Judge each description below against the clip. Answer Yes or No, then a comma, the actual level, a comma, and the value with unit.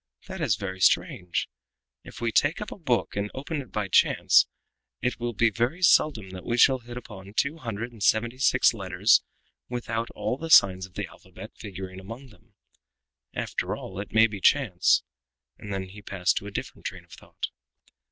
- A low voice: Yes, low, 110 Hz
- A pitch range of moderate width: Yes, average, 4.3 semitones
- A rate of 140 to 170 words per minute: No, average, 190 wpm